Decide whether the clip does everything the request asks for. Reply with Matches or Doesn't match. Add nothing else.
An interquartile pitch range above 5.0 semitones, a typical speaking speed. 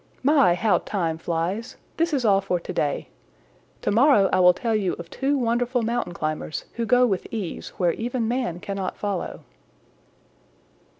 Matches